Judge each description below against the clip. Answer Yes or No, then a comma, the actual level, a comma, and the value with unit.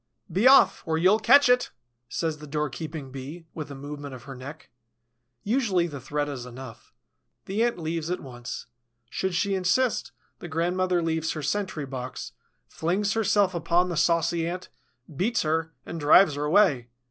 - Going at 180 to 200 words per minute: No, average, 165 wpm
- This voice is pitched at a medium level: Yes, medium, 165 Hz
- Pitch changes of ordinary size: Yes, average, 4.3 semitones